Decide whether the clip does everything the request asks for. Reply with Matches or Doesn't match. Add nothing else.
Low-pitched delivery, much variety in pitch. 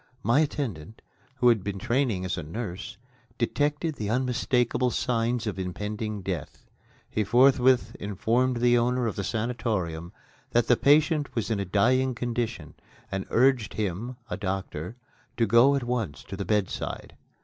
Doesn't match